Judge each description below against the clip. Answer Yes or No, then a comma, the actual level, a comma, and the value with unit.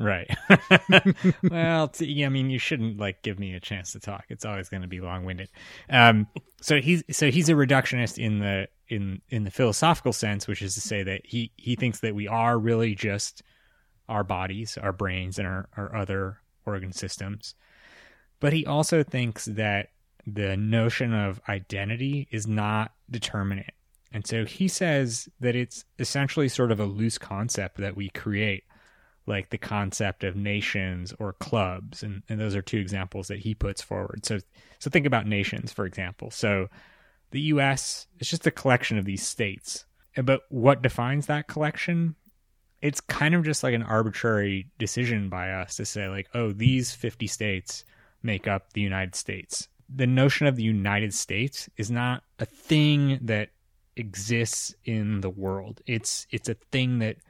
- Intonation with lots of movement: No, average, 4.2 semitones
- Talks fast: No, average, 175 wpm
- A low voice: Yes, low, 110 Hz